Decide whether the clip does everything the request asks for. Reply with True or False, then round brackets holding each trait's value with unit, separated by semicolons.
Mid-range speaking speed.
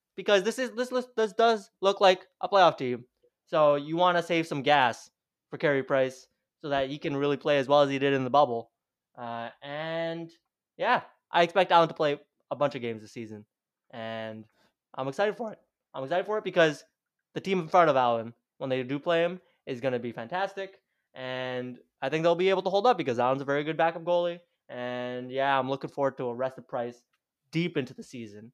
False (220 wpm)